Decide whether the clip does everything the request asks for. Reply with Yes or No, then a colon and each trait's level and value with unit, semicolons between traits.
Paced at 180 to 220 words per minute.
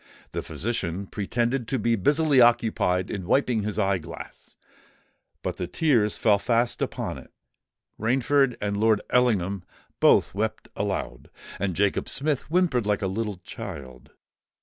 No: slow, 135 wpm